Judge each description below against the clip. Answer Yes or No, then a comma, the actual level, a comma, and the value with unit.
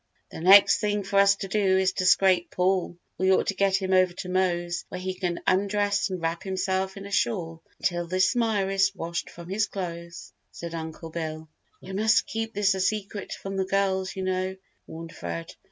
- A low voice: No, high, 190 Hz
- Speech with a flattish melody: Yes, narrow, 2.2 semitones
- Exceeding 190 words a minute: Yes, average, 200 wpm